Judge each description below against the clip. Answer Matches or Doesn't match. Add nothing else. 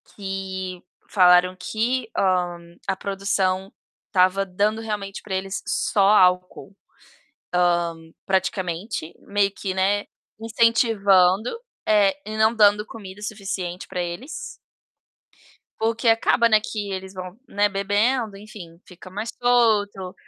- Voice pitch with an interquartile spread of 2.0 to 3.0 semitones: Matches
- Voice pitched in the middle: Doesn't match